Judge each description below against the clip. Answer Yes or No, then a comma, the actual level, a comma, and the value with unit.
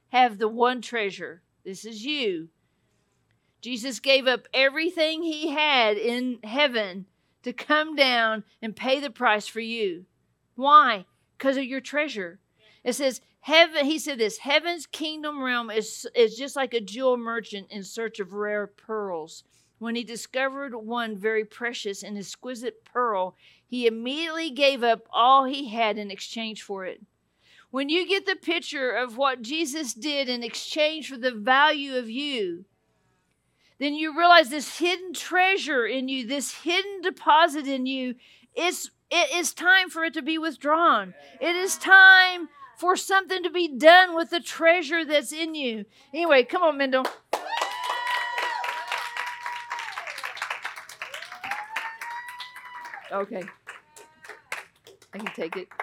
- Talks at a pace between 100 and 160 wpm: Yes, average, 140 wpm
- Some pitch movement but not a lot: No, wide, 6.2 semitones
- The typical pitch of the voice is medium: No, very high, 270 Hz